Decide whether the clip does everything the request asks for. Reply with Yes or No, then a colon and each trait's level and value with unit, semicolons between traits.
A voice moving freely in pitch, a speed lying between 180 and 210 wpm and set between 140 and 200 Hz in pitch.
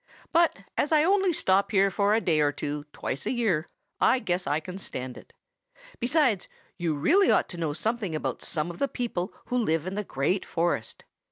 Yes: wide, 7.3 semitones; average, 200 wpm; medium, 185 Hz